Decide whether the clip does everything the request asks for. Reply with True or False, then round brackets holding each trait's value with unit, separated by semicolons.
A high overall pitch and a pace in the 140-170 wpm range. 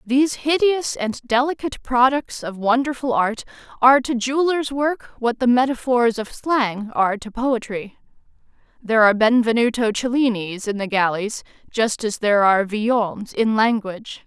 True (235 Hz; 145 wpm)